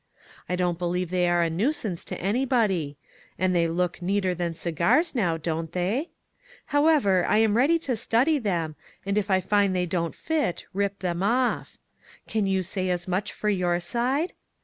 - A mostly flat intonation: No, average, 4.4 semitones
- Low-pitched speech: No, medium, 185 Hz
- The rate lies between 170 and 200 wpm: Yes, average, 175 wpm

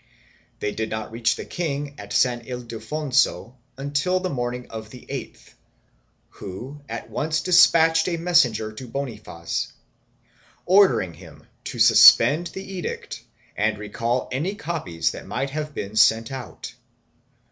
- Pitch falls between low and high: No, low, 130 Hz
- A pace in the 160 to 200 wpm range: No, slow, 135 wpm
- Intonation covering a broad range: Yes, wide, 6.4 semitones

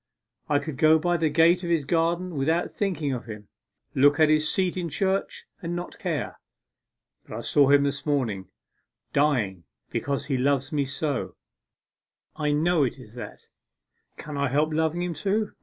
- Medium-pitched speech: Yes, medium, 150 Hz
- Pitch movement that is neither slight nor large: Yes, average, 3.3 semitones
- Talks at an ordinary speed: Yes, average, 175 wpm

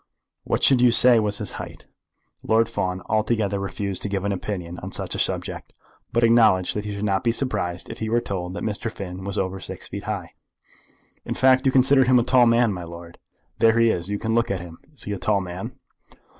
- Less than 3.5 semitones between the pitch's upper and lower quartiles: No, average, 3.8 semitones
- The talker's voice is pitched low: Yes, low, 105 Hz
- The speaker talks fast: Yes, fast, 225 wpm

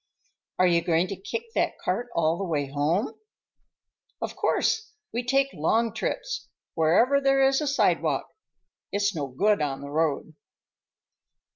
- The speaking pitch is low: No, high, 195 Hz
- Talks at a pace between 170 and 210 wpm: No, average, 145 wpm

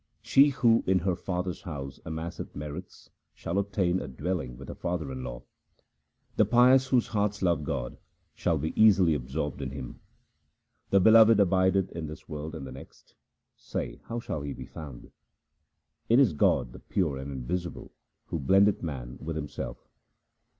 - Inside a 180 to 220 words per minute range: No, average, 165 wpm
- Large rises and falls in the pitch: Yes, wide, 6.0 semitones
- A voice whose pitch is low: Yes, very low, 85 Hz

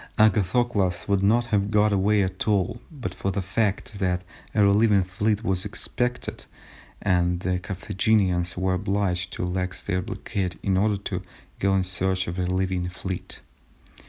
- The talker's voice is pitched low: Yes, very low, 95 Hz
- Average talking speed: Yes, average, 160 wpm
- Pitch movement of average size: No, narrow, 2.2 semitones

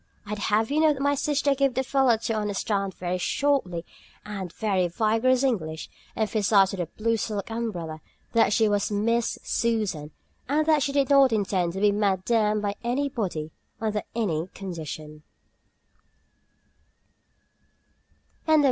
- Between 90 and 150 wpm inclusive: Yes, average, 140 wpm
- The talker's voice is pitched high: Yes, high, 215 Hz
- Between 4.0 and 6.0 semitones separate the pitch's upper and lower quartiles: Yes, average, 4.4 semitones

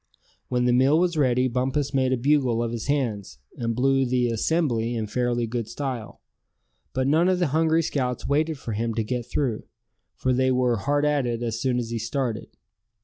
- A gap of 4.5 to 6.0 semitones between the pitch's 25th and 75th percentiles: No, average, 3.2 semitones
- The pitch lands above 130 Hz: No, low, 125 Hz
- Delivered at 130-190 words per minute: No, average, 200 wpm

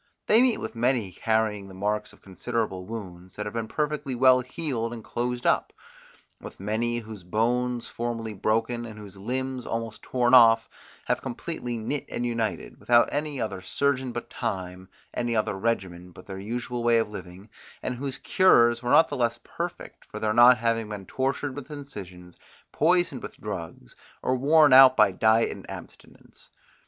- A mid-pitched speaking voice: No, low, 115 Hz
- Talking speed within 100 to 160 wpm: No, average, 170 wpm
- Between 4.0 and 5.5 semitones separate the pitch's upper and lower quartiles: No, average, 3.3 semitones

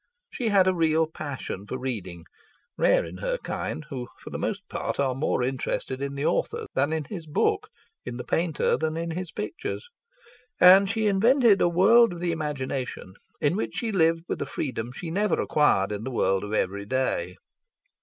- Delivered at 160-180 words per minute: No, average, 190 wpm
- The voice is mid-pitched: Yes, medium, 155 Hz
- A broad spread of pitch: Yes, wide, 6.4 semitones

